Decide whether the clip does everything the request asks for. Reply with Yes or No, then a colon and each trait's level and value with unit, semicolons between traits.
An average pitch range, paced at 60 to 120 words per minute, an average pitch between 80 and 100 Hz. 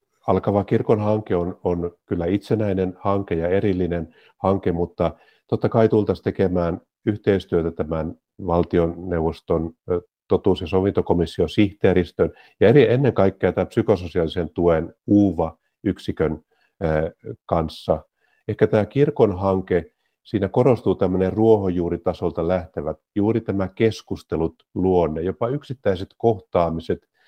Yes: average, 3.0 semitones; average, 105 wpm; very low, 95 Hz